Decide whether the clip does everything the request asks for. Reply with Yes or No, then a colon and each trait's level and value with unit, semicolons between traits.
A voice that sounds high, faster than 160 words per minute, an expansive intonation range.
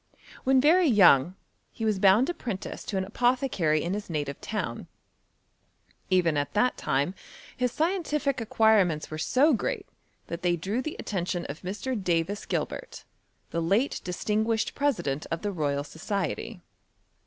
No: high, 200 Hz; average, 140 wpm; wide, 6.7 semitones